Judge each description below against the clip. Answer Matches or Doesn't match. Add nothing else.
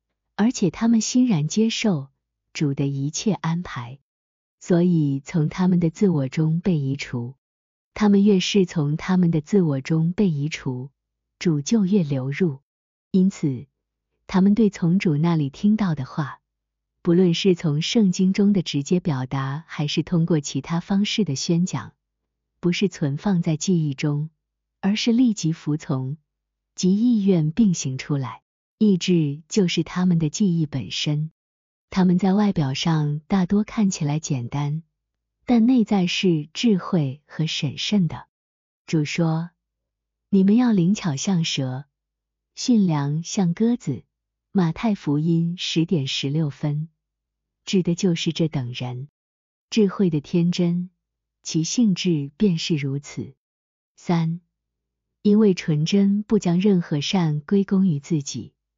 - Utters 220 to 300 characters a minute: Doesn't match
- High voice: Doesn't match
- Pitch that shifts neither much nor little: Matches